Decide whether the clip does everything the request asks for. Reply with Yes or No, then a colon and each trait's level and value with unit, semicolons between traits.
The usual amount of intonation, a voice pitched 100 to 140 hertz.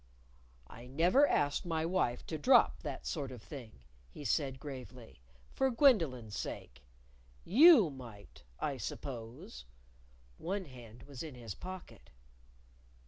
No: wide, 6.4 semitones; low, 135 Hz